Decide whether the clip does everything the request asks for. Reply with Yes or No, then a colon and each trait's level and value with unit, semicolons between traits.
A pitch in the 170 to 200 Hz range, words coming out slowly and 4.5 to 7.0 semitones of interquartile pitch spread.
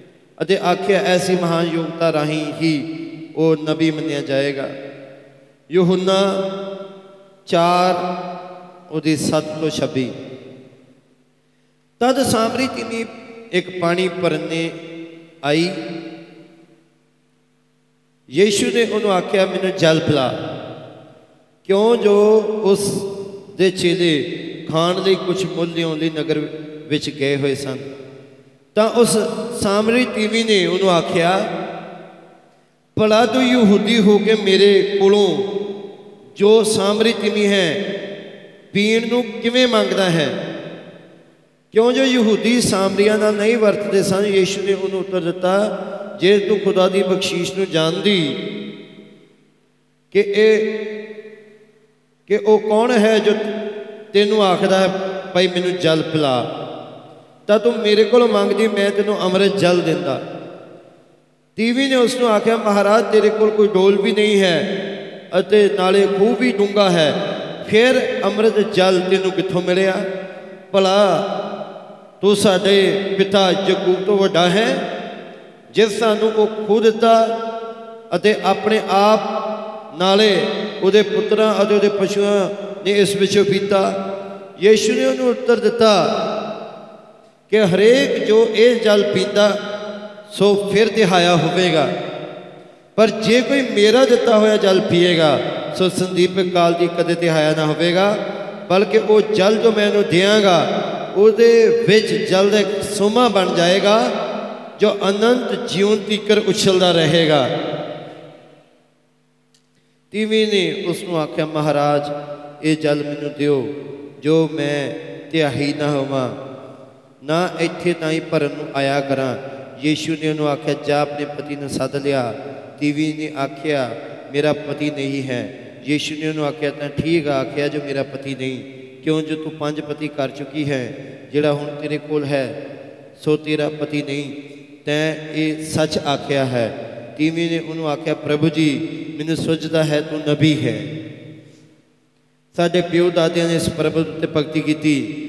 Yes: medium, 185 Hz; slow, 125 wpm; average, 5.2 semitones